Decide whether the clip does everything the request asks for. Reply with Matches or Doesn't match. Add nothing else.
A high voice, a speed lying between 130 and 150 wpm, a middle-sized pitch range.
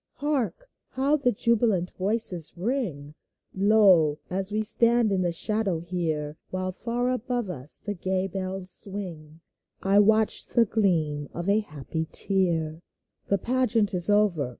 Matches